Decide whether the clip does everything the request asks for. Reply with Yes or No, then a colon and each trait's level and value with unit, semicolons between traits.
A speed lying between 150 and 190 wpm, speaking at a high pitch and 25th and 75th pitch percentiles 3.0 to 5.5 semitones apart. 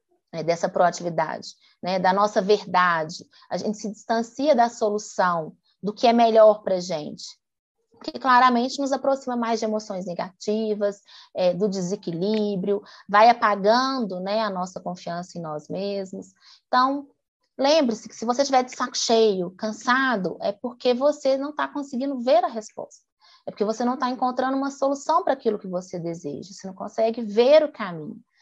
Yes: average, 165 wpm; high, 215 Hz; average, 5.1 semitones